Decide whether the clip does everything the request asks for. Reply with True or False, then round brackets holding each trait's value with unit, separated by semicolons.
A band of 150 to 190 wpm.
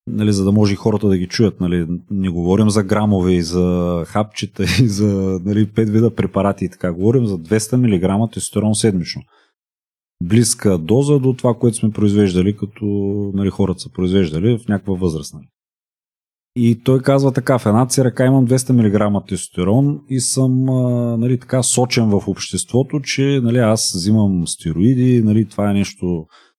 True (165 wpm)